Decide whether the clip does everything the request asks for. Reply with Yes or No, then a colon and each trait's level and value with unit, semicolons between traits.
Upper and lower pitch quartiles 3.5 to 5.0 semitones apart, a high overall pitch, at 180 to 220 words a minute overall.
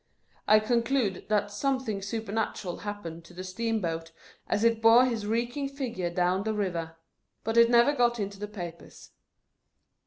No: average, 3.9 semitones; high, 215 Hz; average, 155 wpm